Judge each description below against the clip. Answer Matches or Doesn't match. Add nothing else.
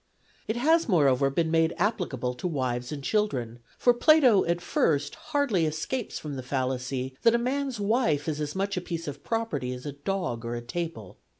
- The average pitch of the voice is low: Doesn't match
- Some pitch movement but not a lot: Doesn't match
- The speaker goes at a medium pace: Matches